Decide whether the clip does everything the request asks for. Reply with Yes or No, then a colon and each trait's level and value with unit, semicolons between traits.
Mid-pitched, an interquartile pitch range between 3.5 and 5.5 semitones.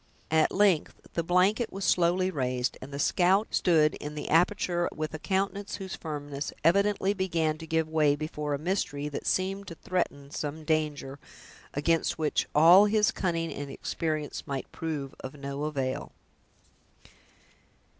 Yes: medium, 160 Hz; average, 4.0 semitones